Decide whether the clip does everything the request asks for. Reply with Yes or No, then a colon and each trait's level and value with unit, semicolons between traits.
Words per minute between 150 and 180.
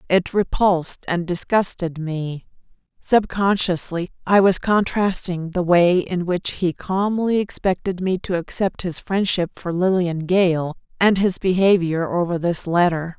No: slow, 135 wpm